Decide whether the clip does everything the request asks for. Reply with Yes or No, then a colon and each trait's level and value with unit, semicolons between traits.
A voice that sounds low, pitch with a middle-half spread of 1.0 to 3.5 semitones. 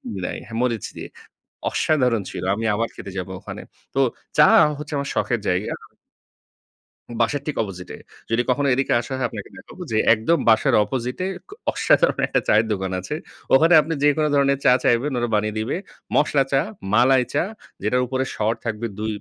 No: low, 120 Hz; average, 4.3 semitones